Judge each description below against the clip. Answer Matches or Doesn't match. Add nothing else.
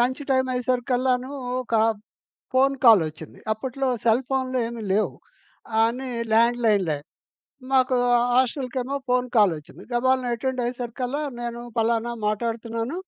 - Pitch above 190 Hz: Matches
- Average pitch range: Doesn't match